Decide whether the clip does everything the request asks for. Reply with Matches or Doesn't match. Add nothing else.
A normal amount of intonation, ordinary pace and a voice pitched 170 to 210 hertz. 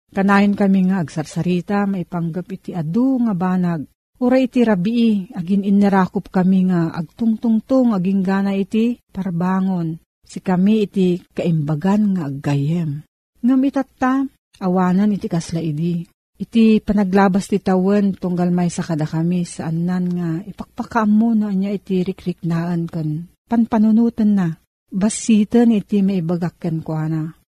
Matches